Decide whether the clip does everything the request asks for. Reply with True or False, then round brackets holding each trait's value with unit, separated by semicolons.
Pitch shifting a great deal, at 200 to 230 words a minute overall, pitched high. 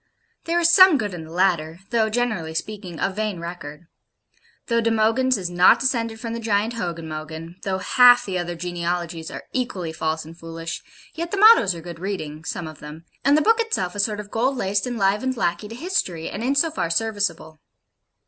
True (5.8 semitones; 205 wpm; 195 Hz)